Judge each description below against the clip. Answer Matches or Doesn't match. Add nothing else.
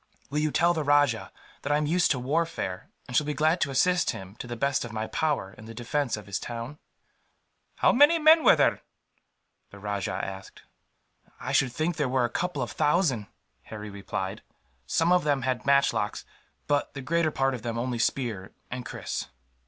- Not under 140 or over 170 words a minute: Doesn't match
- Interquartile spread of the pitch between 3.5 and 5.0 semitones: Doesn't match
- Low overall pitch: Matches